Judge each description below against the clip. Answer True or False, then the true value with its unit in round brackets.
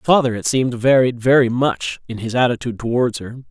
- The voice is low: True (125 Hz)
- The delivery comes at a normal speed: True (190 wpm)